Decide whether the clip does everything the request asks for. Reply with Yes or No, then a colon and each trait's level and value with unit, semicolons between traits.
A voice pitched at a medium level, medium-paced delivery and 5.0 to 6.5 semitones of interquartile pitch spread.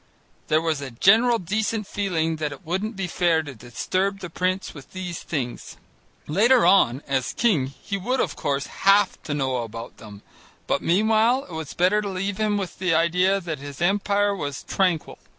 Yes: medium, 180 Hz; average, 185 wpm; wide, 5.5 semitones